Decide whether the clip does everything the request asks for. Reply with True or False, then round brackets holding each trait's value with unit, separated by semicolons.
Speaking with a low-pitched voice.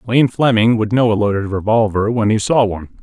True (110 Hz)